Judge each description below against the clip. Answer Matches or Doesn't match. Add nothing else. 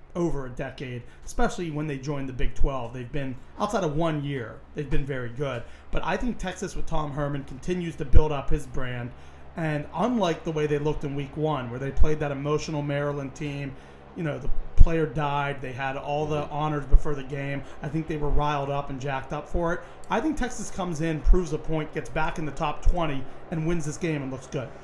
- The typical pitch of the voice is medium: Matches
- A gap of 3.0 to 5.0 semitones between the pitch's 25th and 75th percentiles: Doesn't match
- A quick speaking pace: Matches